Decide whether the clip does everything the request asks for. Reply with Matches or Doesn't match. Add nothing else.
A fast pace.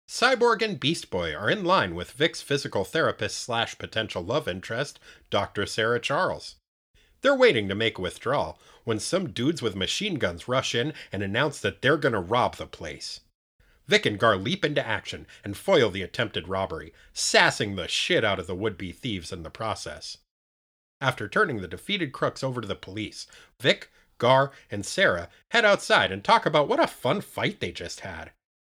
Doesn't match